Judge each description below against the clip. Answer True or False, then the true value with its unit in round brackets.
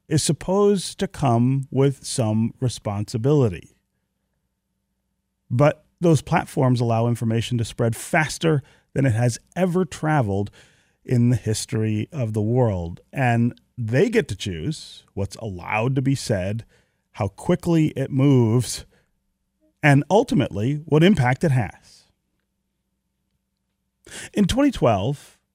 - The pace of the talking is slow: True (115 wpm)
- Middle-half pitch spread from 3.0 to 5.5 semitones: True (5.1 semitones)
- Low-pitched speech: True (130 Hz)